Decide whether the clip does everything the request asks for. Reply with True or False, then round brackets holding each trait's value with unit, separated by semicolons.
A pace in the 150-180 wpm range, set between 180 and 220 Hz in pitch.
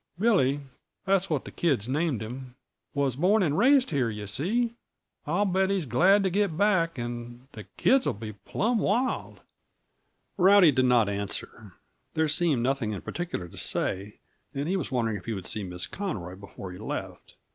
False (175 wpm; 140 Hz)